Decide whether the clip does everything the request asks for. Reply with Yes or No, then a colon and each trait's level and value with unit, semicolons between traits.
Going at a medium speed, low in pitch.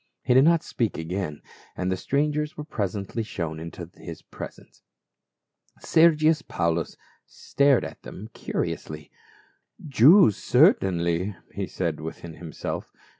No: slow, 120 wpm; very low, 95 Hz